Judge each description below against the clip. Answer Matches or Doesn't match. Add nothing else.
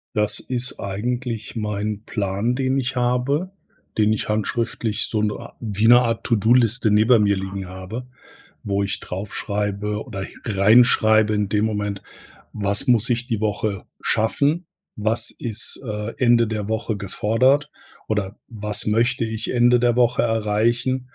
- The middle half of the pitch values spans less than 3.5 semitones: Matches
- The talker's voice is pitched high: Doesn't match